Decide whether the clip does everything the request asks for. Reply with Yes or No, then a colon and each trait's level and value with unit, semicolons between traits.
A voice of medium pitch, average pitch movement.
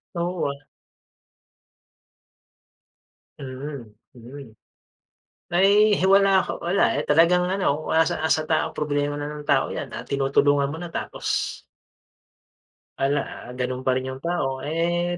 Yes: medium, 150 Hz; average, 3.8 semitones